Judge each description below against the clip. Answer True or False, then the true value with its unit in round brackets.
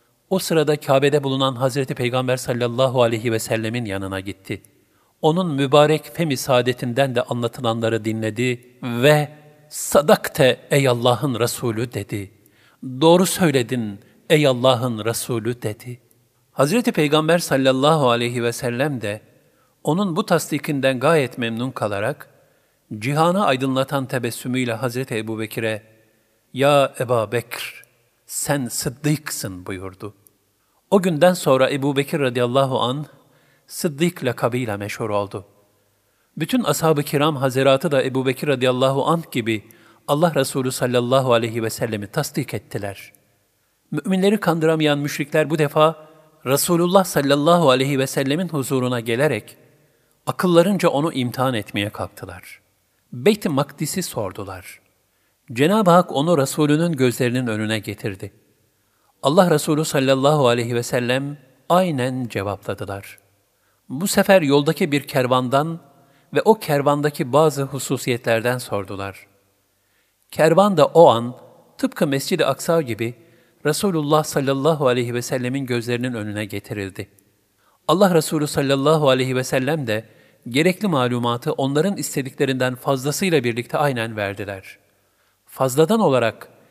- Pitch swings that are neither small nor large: True (4.6 semitones)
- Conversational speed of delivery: True (115 wpm)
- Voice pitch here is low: True (130 Hz)